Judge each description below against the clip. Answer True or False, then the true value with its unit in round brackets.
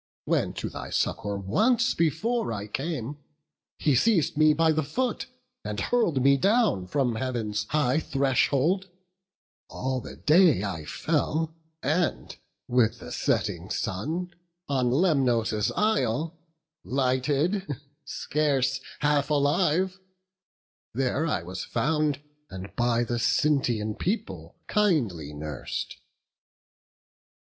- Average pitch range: False (5.7 semitones)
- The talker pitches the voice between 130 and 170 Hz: True (140 Hz)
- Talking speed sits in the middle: False (110 wpm)